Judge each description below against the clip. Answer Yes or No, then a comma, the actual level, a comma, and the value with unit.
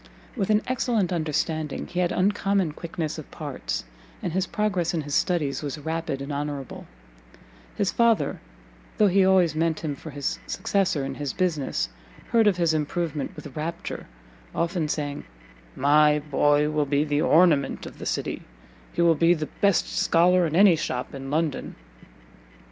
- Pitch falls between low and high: Yes, medium, 160 Hz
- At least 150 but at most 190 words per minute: Yes, average, 160 wpm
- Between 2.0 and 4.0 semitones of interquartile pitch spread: Yes, average, 3.6 semitones